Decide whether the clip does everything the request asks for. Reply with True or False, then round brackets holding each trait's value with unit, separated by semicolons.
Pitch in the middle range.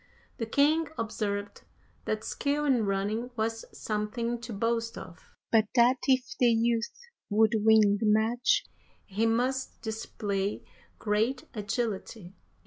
False (225 Hz)